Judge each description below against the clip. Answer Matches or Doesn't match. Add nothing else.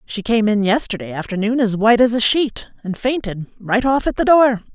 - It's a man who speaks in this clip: Doesn't match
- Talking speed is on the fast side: Matches